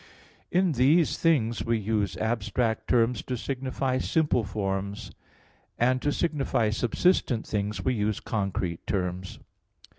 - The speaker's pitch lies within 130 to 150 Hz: No, low, 115 Hz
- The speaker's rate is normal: No, slow, 120 wpm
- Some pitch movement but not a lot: Yes, average, 4.0 semitones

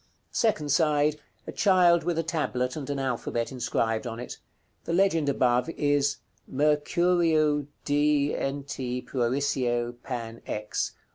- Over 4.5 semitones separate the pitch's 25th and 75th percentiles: No, average, 3.8 semitones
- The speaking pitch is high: No, medium, 145 Hz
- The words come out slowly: Yes, slow, 120 wpm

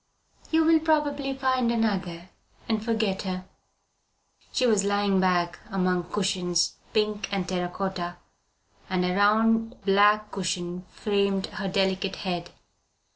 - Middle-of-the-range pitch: No, high, 195 Hz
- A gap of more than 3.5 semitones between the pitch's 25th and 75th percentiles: No, average, 3.2 semitones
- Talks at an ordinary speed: No, slow, 125 wpm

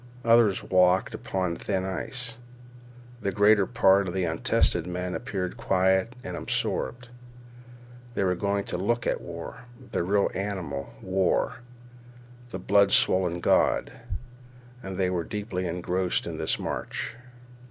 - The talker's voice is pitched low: Yes, very low, 95 Hz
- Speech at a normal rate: No, slow, 130 wpm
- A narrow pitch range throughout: Yes, narrow, 2.3 semitones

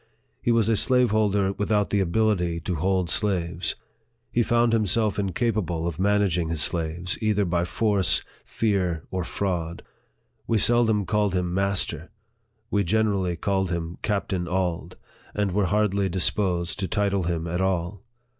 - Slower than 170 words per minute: Yes, average, 155 wpm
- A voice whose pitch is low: Yes, very low, 95 Hz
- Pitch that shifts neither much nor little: Yes, average, 3.3 semitones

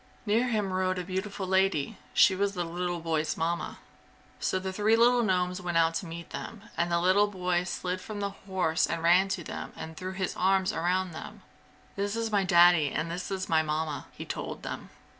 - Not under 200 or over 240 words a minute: Yes, fast, 205 wpm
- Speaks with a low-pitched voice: No, medium, 185 Hz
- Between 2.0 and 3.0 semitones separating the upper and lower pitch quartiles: Yes, narrow, 2.4 semitones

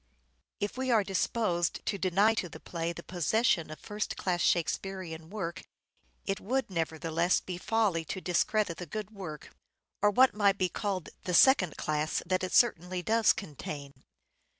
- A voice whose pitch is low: No, medium, 185 Hz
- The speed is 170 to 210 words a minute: Yes, average, 175 wpm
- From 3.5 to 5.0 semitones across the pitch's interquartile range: Yes, average, 4.0 semitones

